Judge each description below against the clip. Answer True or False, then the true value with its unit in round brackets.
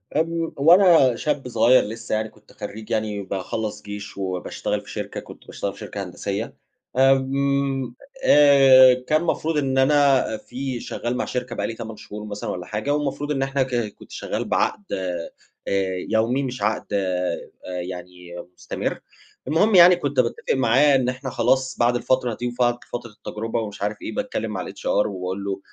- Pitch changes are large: False (4.6 semitones)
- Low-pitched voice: True (125 Hz)